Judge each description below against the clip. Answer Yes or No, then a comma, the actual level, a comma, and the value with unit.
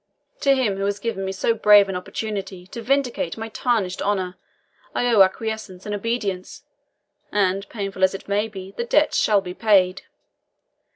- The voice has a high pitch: Yes, high, 200 Hz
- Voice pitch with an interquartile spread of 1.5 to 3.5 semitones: Yes, average, 2.8 semitones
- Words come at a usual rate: Yes, average, 170 wpm